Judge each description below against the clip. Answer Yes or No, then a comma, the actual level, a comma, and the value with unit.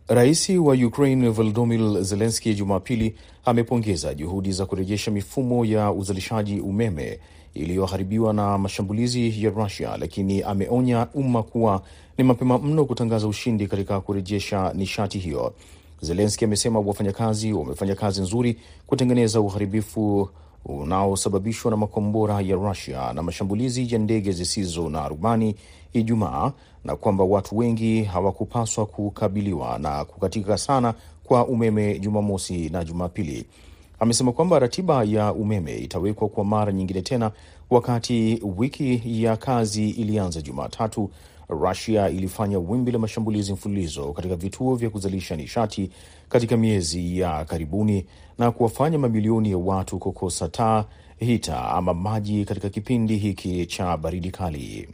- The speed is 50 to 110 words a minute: No, average, 125 wpm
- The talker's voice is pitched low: Yes, low, 105 Hz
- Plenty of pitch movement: No, average, 3.3 semitones